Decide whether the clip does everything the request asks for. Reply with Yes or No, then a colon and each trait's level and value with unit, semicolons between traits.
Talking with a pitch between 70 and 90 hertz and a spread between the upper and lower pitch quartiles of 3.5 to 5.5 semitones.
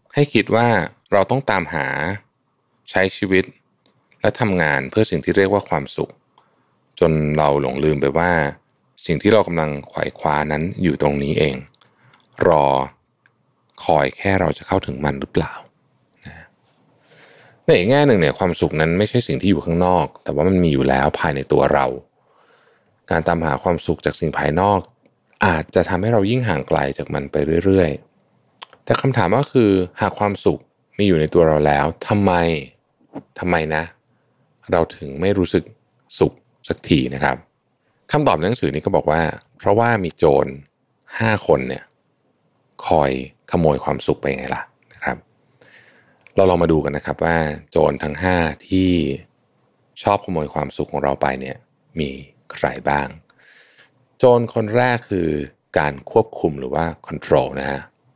Yes: very low, 85 Hz; average, 5.1 semitones